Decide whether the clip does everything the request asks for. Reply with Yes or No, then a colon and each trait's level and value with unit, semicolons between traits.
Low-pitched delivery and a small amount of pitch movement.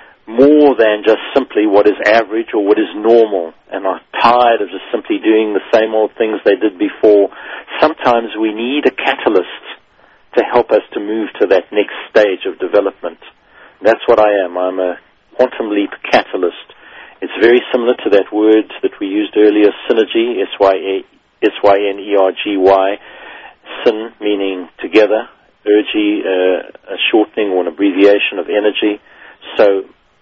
No: low, 110 Hz; average, 3.6 semitones